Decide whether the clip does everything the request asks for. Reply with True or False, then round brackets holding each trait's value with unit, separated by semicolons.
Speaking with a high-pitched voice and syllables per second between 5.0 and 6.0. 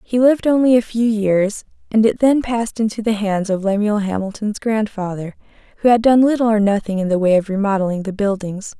True (210 Hz; 5.7 syllables/s)